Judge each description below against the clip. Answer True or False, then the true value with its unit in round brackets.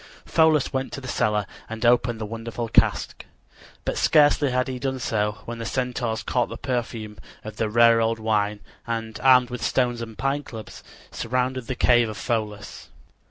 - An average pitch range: False (2.3 semitones)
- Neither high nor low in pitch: False (120 Hz)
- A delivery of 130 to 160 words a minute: False (175 wpm)